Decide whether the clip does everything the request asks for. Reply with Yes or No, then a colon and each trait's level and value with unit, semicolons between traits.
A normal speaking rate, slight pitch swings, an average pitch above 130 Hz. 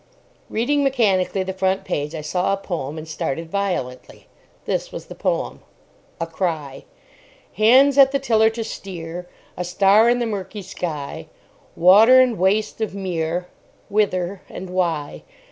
No: average, 145 wpm; average, 4.6 semitones; high, 190 Hz